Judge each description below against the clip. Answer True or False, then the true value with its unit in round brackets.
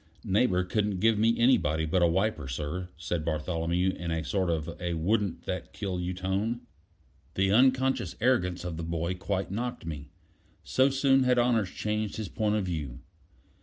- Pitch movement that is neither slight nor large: True (4.6 semitones)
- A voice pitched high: False (95 Hz)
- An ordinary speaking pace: True (170 wpm)